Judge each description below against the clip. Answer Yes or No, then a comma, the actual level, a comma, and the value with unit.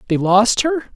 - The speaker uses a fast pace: No, average, 190 wpm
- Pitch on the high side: Yes, high, 230 Hz